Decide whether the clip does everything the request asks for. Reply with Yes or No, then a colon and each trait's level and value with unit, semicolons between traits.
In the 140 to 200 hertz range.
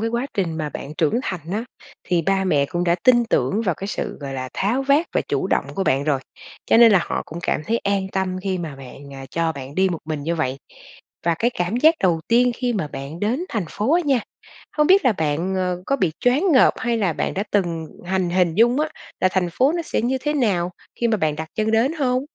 Yes: high, 190 Hz